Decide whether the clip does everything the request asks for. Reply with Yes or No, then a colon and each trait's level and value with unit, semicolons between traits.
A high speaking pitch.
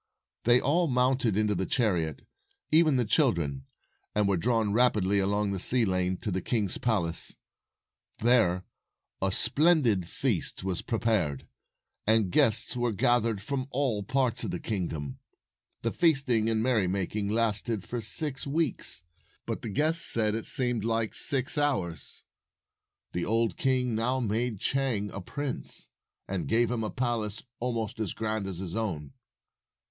No: low, 110 Hz